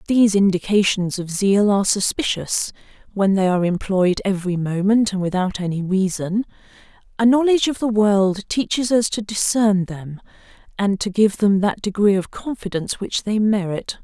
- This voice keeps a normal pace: Yes, average, 160 wpm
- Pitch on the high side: Yes, high, 200 Hz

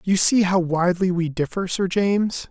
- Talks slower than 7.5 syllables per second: Yes, 5.0 syllables/s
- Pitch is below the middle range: No, medium, 185 Hz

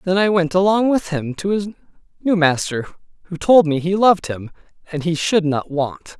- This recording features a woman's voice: No, male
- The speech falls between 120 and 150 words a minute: No, fast, 205 wpm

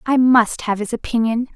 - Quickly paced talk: No, average, 195 wpm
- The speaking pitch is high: Yes, high, 235 Hz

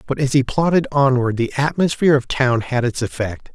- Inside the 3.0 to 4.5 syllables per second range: No, 5.4 syllables/s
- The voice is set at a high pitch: No, low, 130 Hz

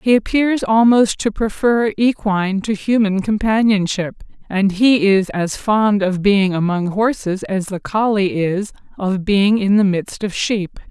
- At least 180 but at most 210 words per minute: No, average, 160 wpm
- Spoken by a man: No, female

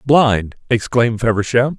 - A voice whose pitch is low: Yes, low, 120 Hz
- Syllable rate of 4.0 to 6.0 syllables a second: Yes, 4.6 syllables/s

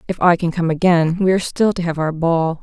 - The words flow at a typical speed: No, fast, 275 wpm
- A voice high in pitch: No, medium, 170 Hz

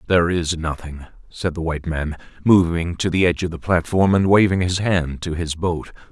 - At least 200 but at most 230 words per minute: Yes, fast, 205 wpm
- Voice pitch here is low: Yes, very low, 85 Hz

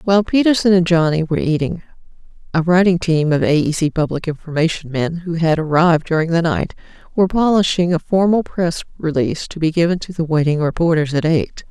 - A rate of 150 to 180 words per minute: No, average, 190 wpm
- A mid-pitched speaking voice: Yes, medium, 165 Hz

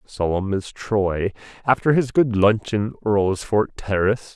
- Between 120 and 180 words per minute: Yes, average, 140 wpm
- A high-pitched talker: No, low, 105 Hz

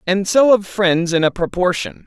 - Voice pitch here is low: No, medium, 185 Hz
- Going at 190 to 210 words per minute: Yes, fast, 205 wpm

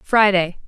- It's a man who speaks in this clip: No, female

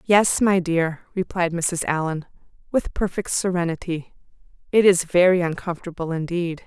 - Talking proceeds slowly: Yes, slow, 125 wpm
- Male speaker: No, female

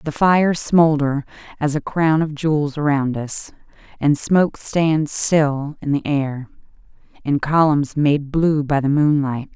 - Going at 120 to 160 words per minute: Yes, average, 150 wpm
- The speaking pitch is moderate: Yes, medium, 150 Hz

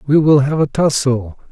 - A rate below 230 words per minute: Yes, average, 200 wpm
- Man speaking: Yes, male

